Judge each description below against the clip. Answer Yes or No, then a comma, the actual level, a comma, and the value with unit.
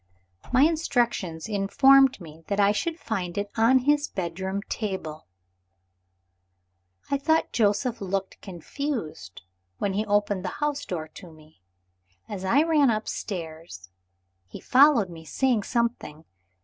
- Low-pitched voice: No, high, 205 Hz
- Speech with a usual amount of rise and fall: No, wide, 6.8 semitones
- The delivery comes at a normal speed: No, slow, 125 wpm